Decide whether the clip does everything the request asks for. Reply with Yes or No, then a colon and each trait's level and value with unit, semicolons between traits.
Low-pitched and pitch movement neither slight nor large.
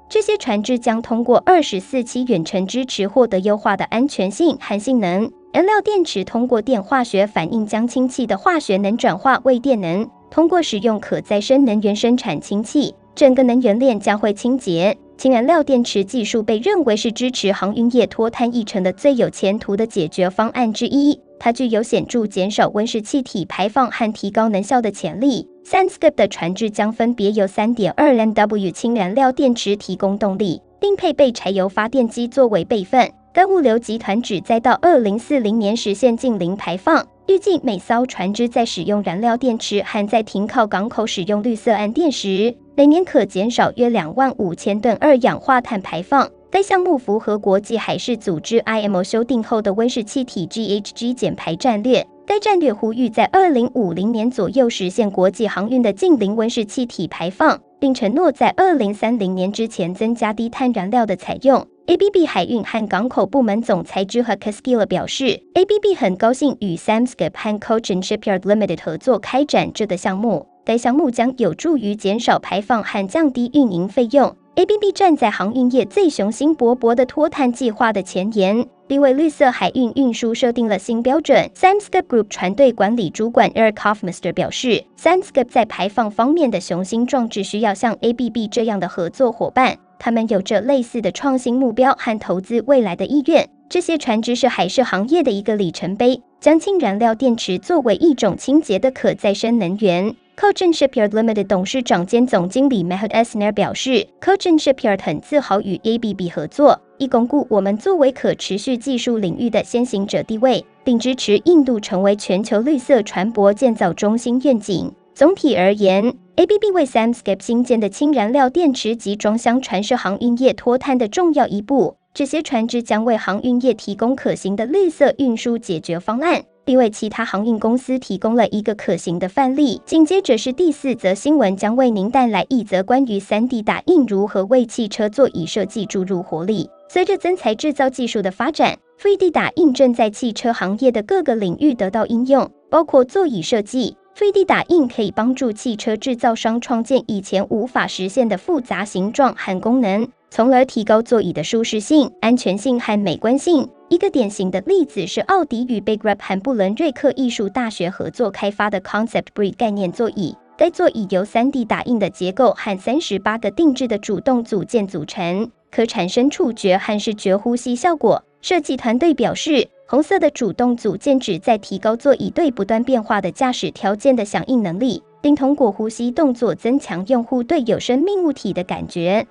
No: high, 230 Hz; average, 4.5 semitones